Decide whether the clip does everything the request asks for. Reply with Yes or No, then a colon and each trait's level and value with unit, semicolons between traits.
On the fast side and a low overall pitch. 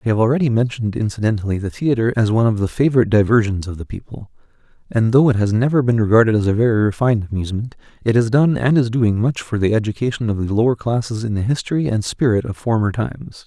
Yes: fast, 225 wpm; low, 115 Hz